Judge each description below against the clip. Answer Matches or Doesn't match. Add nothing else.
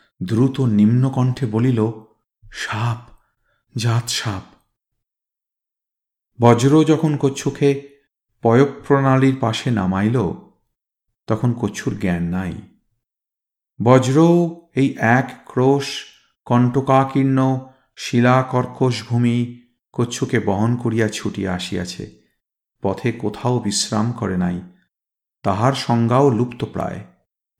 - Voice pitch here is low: Matches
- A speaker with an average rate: Matches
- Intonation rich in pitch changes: Doesn't match